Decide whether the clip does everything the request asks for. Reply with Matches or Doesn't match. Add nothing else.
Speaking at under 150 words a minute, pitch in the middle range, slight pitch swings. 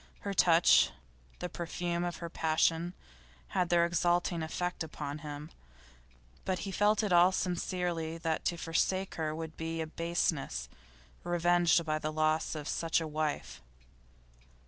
Matches